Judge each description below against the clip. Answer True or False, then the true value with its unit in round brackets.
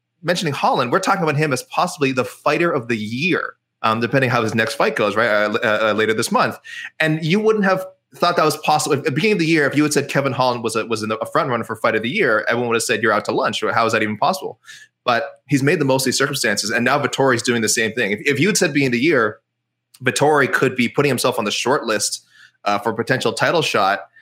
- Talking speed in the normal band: False (275 wpm)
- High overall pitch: False (135 Hz)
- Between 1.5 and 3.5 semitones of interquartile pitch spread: False (4.4 semitones)